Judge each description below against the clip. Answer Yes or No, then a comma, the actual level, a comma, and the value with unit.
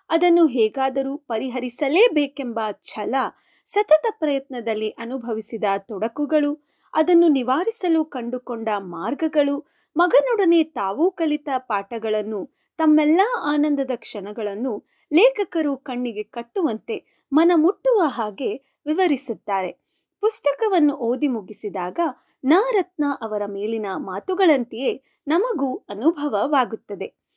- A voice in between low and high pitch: No, very high, 280 Hz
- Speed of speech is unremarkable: Yes, average, 75 wpm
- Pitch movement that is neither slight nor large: No, wide, 6.4 semitones